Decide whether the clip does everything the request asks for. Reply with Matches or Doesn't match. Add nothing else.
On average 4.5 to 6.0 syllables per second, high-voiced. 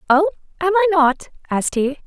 Matches